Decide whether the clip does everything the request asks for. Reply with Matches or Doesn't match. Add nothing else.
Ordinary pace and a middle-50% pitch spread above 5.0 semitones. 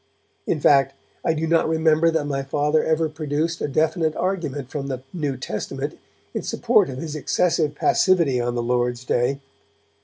Doesn't match